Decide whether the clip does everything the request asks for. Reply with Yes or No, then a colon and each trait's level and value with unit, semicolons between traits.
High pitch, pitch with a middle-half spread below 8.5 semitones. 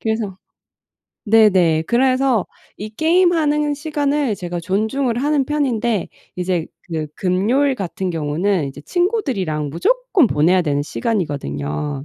No: high, 210 Hz; wide, 8.8 semitones